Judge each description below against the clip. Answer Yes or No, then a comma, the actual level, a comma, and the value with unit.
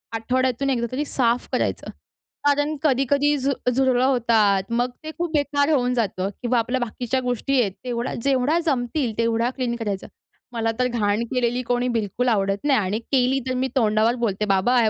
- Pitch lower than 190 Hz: No, high, 245 Hz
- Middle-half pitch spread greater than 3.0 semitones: No, average, 2.7 semitones